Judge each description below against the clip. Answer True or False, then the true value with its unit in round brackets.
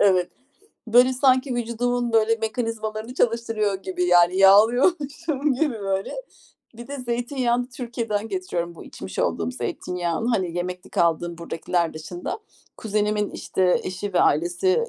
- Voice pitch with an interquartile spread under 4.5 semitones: False (5.4 semitones)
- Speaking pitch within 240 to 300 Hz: False (215 Hz)